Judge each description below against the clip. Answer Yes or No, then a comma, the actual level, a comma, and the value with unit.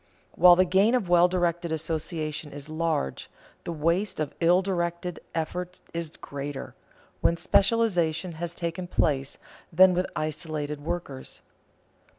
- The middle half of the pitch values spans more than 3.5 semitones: No, narrow, 2.5 semitones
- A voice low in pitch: No, medium, 170 Hz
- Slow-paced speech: Yes, slow, 130 wpm